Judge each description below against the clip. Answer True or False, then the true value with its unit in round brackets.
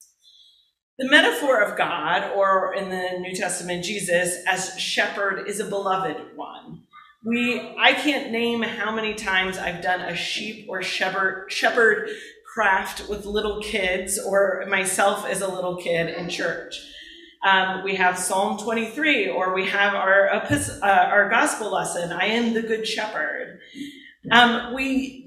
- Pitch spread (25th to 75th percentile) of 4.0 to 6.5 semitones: False (3.5 semitones)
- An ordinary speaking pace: True (145 wpm)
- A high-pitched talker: True (195 Hz)